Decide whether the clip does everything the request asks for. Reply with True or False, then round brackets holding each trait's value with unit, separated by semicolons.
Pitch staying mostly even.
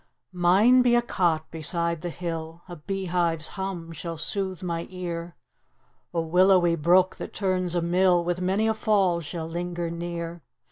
True (1.9 semitones)